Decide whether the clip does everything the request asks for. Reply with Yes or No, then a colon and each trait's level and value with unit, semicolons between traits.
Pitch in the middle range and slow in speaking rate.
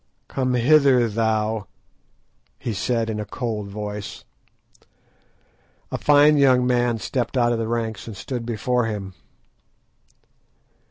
No: low, 115 Hz; slow, 120 wpm